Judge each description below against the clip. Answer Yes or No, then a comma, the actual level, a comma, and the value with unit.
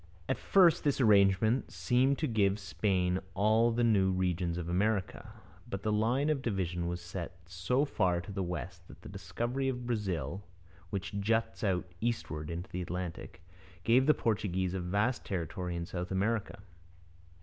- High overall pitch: No, low, 100 Hz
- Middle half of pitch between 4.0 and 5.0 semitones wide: Yes, average, 4.4 semitones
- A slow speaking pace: No, average, 160 wpm